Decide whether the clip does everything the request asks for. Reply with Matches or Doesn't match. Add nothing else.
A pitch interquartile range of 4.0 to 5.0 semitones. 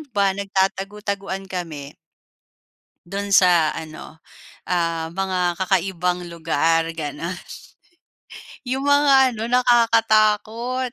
Matches